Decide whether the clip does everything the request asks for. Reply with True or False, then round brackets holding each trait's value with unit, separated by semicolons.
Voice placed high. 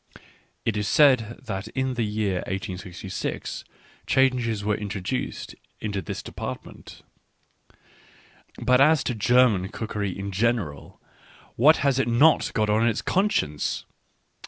False (110 Hz)